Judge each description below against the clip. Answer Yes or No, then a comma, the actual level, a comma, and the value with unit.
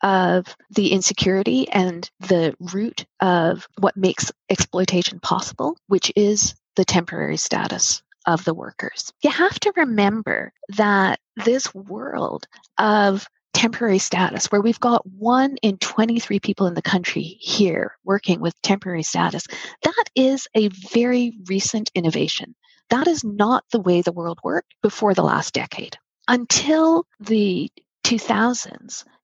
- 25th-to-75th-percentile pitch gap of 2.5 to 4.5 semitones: Yes, average, 3.9 semitones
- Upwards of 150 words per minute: No, slow, 135 wpm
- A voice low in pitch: No, high, 205 Hz